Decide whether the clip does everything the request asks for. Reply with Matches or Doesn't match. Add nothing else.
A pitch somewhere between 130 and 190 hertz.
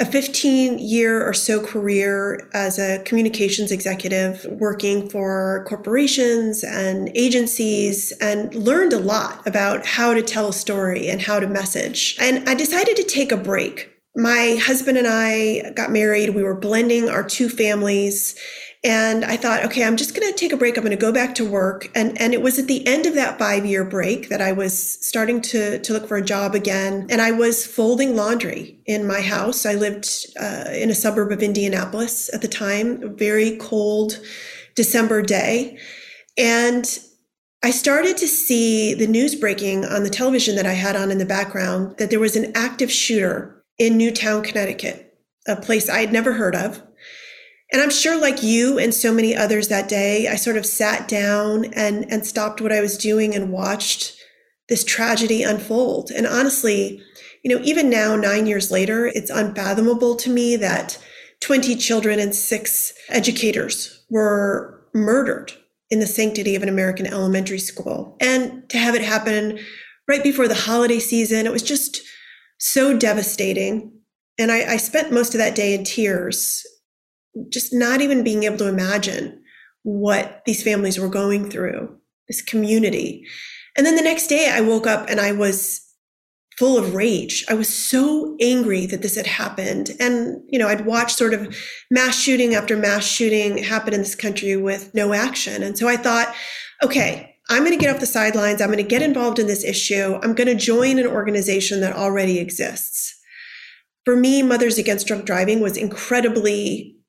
Doesn't match